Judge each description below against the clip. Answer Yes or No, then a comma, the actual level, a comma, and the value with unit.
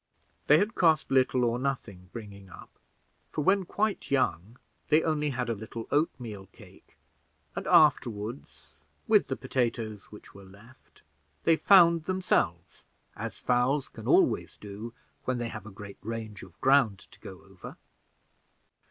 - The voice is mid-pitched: No, low, 120 Hz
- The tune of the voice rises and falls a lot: Yes, wide, 6.0 semitones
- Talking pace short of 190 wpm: Yes, average, 145 wpm